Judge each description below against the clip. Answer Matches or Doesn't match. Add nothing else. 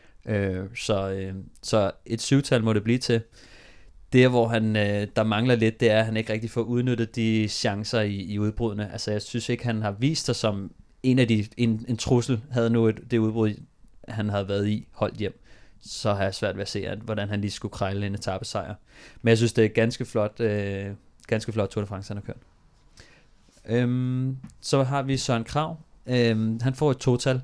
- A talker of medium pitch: Doesn't match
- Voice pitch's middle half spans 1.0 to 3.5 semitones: Matches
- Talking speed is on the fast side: Doesn't match